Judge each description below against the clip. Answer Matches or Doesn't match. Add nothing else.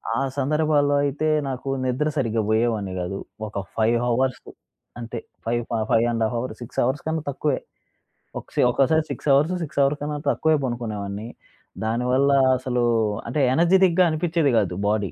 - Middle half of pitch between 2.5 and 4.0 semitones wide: Doesn't match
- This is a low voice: Matches